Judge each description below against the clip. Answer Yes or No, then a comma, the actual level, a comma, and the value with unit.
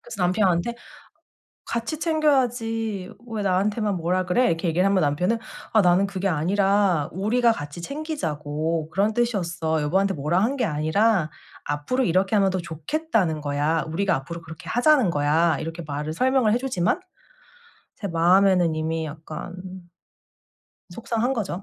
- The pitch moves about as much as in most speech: No, wide, 5.7 semitones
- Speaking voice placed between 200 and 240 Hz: No, medium, 185 Hz